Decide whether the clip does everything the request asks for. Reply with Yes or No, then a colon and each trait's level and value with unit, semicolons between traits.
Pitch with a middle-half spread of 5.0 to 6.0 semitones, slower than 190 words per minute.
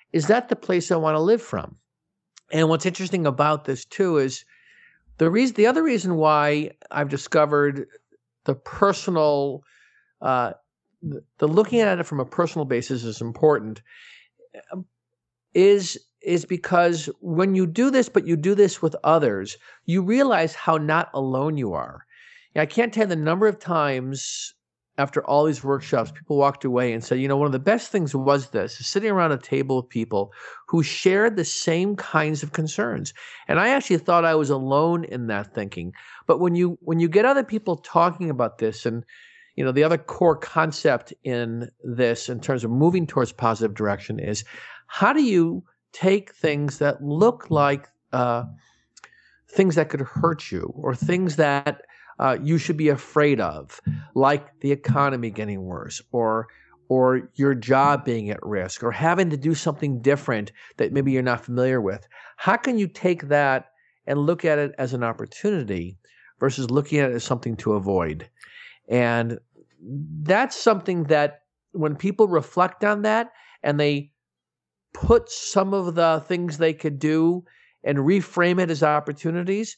Yes: wide, 5.4 semitones; average, 170 wpm